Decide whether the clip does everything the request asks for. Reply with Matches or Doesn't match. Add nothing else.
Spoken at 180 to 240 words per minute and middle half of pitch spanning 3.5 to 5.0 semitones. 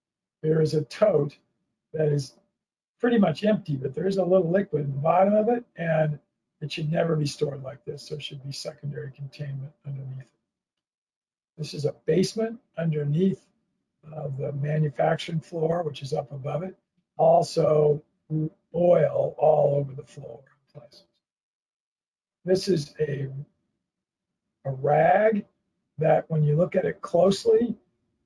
Doesn't match